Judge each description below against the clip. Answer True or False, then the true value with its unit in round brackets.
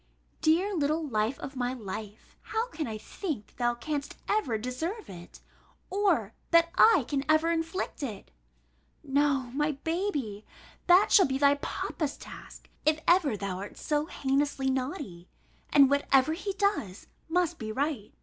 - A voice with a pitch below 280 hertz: False (285 Hz)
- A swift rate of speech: False (150 wpm)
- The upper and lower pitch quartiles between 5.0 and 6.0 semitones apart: True (5.6 semitones)